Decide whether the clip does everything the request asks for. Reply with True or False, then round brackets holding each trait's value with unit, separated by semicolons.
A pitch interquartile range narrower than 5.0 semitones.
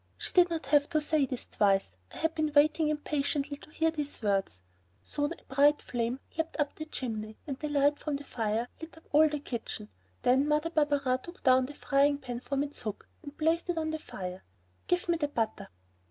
True (3.5 semitones)